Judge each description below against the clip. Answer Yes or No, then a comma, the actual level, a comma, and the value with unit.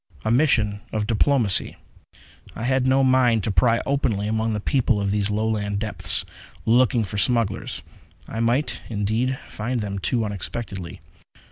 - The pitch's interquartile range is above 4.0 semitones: No, average, 3.2 semitones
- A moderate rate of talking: Yes, average, 145 wpm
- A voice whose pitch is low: Yes, low, 110 Hz